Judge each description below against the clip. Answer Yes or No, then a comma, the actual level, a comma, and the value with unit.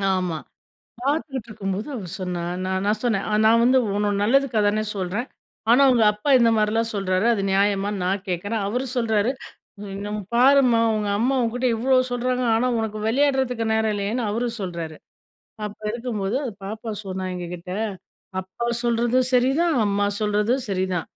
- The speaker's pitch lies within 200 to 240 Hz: Yes, high, 220 Hz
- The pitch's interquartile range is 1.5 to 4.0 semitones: Yes, average, 3.7 semitones